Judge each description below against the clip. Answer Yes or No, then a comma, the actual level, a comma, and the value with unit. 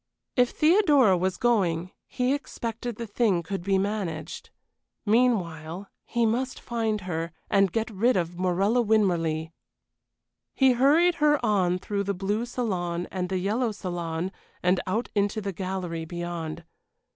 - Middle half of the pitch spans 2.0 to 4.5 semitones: No, average, 4.9 semitones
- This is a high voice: Yes, high, 195 Hz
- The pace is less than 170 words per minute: Yes, average, 140 wpm